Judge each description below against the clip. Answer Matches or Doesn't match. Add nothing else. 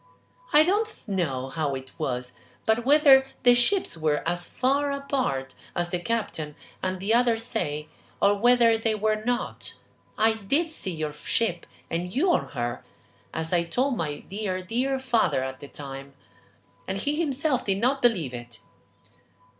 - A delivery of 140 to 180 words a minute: Matches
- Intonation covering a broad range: Matches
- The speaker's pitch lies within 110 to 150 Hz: Doesn't match